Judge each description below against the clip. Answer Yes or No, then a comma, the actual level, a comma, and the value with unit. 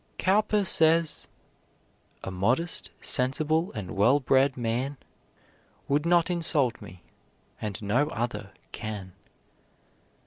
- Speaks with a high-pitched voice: No, low, 135 Hz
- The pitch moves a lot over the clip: Yes, wide, 6.9 semitones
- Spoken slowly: Yes, slow, 100 wpm